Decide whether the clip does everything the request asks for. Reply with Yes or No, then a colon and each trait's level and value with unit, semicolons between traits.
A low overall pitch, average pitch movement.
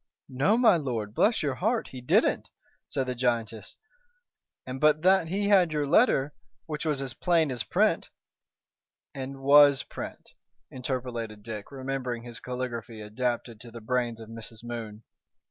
Yes: low, 130 Hz; average, 4.2 semitones